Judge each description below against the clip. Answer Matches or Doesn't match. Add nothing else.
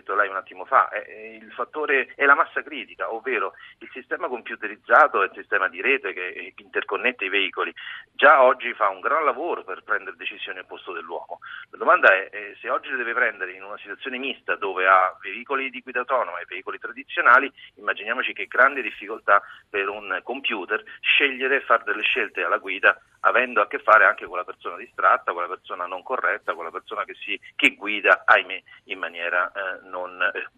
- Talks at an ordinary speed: Doesn't match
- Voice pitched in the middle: Matches